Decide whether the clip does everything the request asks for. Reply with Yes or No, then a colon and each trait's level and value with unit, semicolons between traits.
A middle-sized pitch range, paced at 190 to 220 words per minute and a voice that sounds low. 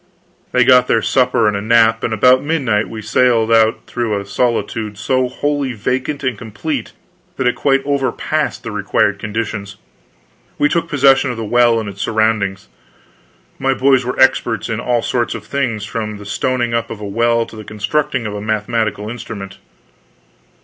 No: average, 3.2 semitones; average, 175 wpm; low, 115 Hz